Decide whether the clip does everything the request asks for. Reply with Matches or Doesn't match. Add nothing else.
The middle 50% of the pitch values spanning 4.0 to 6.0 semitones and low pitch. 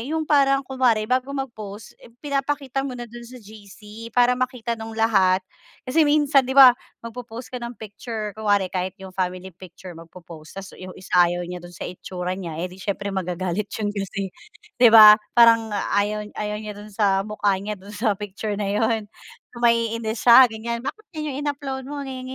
Doesn't match